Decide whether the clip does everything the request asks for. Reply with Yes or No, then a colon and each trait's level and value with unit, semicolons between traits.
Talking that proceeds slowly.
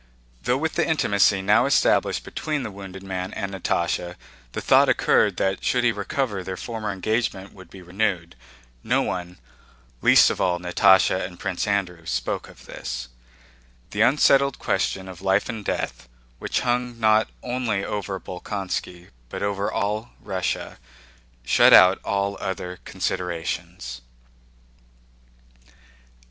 Yes: slow, 130 wpm